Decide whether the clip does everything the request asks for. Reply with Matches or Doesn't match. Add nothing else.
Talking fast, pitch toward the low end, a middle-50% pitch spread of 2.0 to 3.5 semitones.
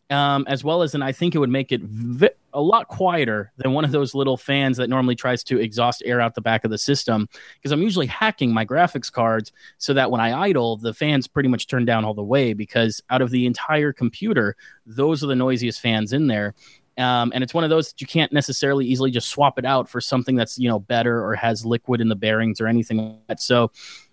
Matches